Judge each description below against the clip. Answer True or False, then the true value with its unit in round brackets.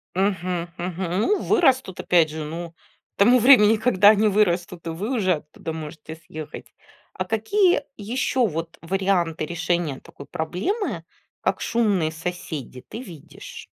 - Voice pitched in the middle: True (180 Hz)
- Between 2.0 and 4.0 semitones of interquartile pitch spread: False (4.9 semitones)